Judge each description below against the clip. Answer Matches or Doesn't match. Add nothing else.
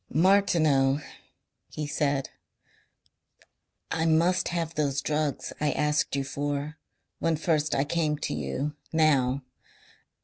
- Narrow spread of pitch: Matches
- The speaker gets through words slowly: Matches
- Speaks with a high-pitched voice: Doesn't match